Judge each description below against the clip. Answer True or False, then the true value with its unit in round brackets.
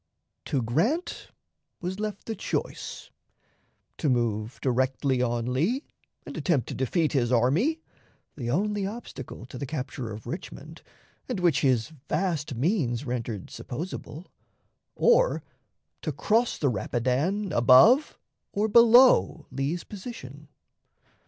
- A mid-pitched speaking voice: True (145 Hz)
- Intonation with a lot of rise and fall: True (8.6 semitones)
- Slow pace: True (120 wpm)